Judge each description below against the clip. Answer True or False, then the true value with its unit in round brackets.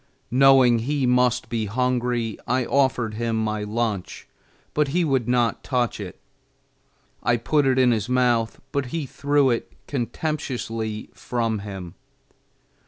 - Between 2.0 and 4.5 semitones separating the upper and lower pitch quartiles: True (2.8 semitones)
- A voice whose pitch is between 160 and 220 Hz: False (120 Hz)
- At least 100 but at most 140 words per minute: True (135 wpm)